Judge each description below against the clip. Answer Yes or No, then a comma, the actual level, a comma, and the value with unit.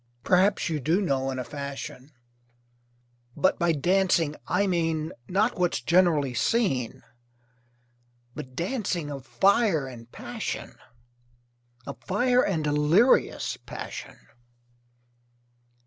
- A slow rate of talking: Yes, slow, 100 wpm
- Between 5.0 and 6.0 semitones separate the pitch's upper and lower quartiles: Yes, wide, 5.4 semitones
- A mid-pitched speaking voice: Yes, medium, 165 Hz